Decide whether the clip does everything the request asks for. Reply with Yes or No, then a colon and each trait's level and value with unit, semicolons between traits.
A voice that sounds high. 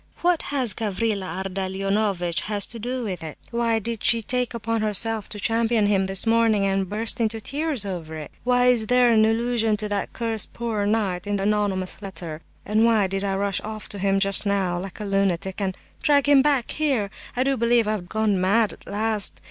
Yes: high, 210 Hz